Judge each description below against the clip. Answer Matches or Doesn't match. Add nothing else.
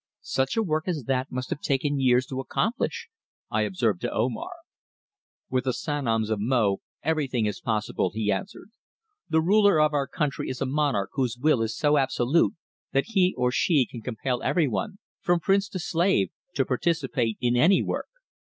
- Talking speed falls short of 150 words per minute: Doesn't match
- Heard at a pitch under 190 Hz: Matches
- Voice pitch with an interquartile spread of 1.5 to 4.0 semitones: Doesn't match